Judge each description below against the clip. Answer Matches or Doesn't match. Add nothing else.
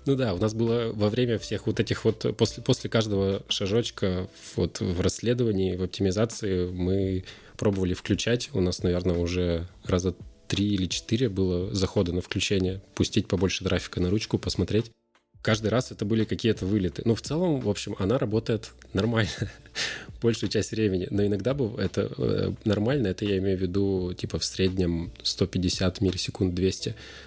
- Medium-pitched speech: Doesn't match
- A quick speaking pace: Matches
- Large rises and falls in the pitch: Doesn't match